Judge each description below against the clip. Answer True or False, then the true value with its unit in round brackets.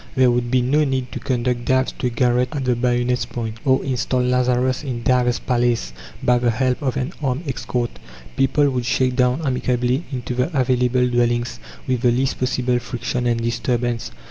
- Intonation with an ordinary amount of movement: False (1.1 semitones)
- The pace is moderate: True (185 wpm)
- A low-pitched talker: True (125 Hz)